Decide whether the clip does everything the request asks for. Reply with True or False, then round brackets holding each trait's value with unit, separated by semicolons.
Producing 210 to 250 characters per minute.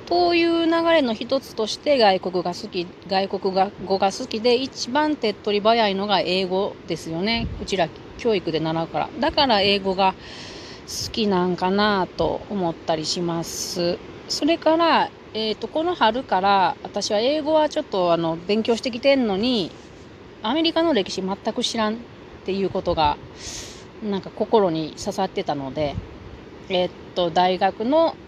False (295 characters per minute)